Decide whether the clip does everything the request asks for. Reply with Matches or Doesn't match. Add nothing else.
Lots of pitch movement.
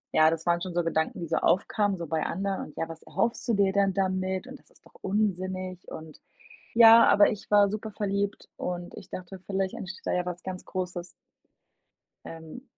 Doesn't match